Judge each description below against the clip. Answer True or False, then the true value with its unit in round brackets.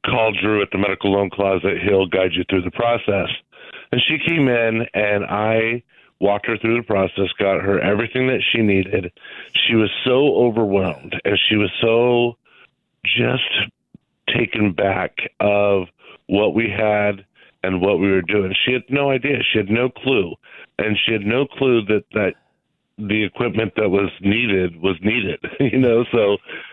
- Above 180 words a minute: False (170 wpm)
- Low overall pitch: True (105 Hz)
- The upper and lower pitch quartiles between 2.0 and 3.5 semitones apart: True (3.1 semitones)